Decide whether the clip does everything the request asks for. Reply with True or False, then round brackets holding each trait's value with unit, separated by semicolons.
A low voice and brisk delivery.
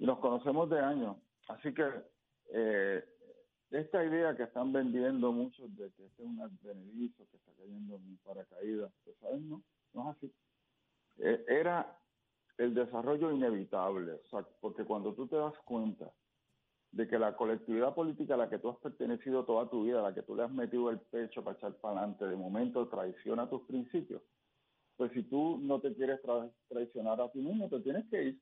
True (125 Hz; 195 wpm)